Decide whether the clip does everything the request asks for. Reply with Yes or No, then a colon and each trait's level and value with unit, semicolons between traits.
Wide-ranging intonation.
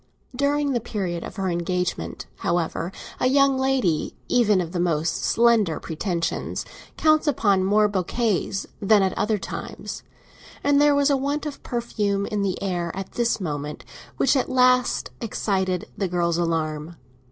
Yes: wide, 6.3 semitones